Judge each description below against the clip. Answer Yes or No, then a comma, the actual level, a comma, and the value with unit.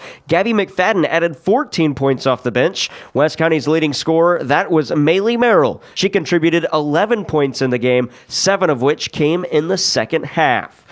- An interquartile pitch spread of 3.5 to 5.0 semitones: Yes, average, 3.8 semitones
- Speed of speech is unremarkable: Yes, average, 170 wpm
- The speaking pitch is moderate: Yes, medium, 160 Hz